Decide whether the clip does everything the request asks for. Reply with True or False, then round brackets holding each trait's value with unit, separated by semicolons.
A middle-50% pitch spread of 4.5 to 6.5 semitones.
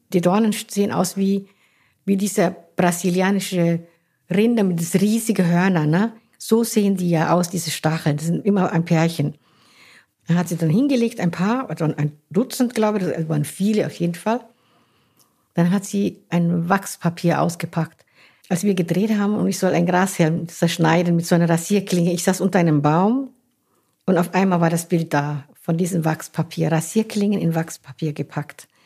False (3.3 semitones)